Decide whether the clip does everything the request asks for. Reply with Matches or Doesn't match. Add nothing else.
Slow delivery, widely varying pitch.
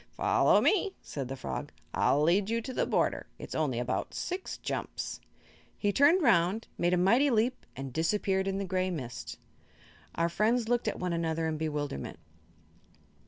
Doesn't match